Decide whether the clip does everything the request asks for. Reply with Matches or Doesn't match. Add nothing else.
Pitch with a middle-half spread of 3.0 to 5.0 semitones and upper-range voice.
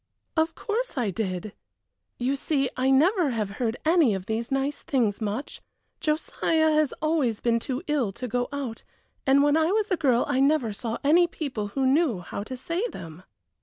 Doesn't match